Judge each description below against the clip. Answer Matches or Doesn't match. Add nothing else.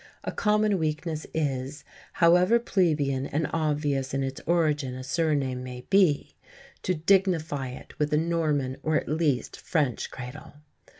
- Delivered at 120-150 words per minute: Matches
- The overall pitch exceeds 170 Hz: Doesn't match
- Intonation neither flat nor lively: Matches